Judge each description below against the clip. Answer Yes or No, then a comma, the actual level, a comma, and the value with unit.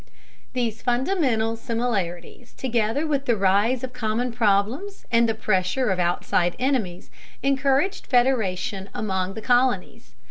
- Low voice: No, high, 230 Hz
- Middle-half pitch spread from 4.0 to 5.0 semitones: Yes, average, 4.6 semitones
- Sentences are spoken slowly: Yes, slow, 120 wpm